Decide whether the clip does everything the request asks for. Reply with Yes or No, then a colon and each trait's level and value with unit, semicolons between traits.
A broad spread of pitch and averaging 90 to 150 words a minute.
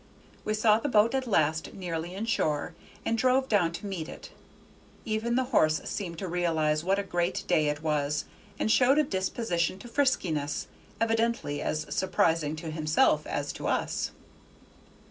No: wide, 6.2 semitones; average, 165 wpm